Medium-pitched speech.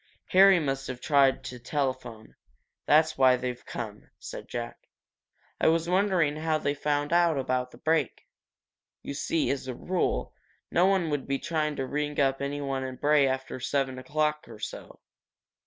Yes: medium, 145 Hz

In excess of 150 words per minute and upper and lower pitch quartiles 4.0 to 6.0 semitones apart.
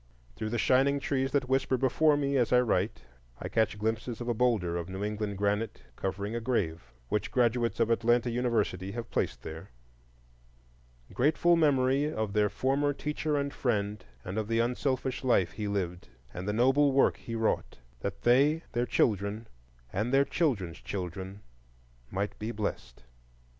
Yes: average, 165 wpm; average, 4.4 semitones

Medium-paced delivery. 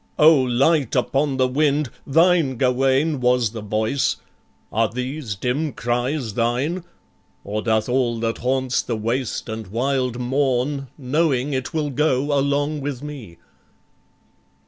No: slow, 130 wpm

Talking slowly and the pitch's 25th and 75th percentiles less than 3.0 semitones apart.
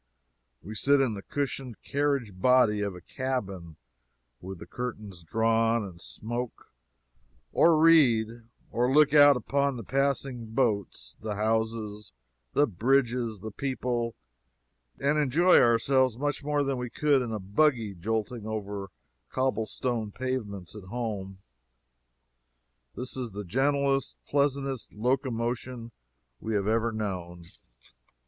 No: slow, 125 wpm; average, 4.3 semitones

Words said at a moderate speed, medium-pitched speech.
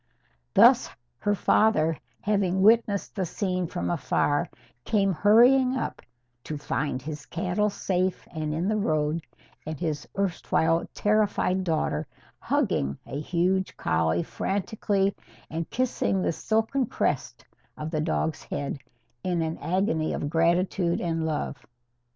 No: slow, 125 wpm; medium, 175 Hz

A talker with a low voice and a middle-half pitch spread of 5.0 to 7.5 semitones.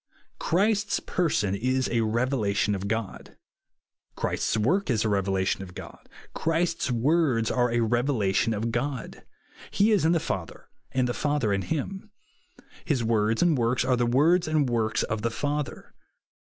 Yes: low, 120 Hz; wide, 5.5 semitones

